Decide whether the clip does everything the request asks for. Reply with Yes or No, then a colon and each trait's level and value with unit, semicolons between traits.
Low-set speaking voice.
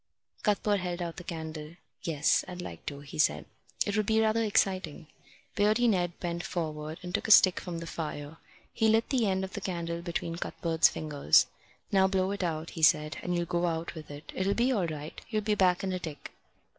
No: medium, 175 Hz